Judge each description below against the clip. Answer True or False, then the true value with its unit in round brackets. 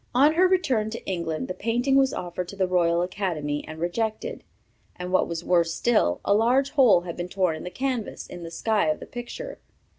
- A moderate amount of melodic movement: False (5.9 semitones)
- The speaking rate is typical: False (210 wpm)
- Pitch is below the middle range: False (190 Hz)